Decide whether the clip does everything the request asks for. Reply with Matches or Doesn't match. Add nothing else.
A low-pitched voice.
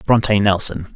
Matches